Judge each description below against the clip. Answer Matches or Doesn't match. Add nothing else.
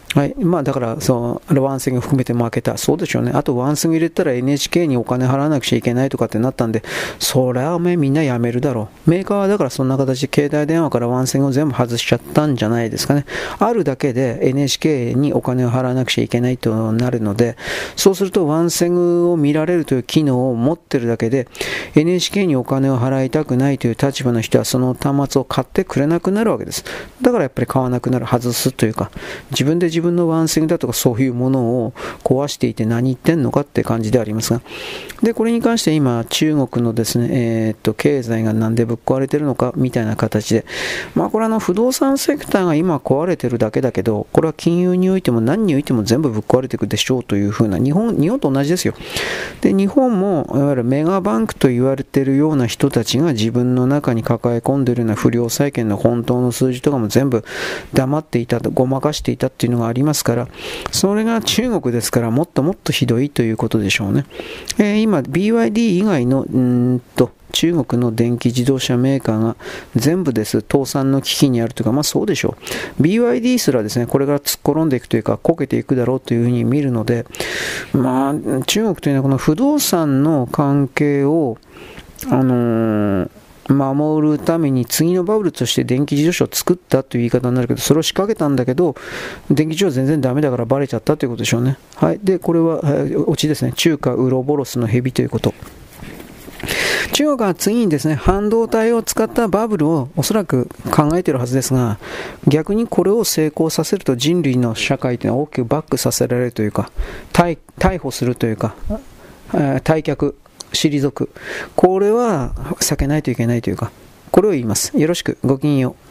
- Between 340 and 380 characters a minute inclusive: Doesn't match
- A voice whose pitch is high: Doesn't match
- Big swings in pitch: Doesn't match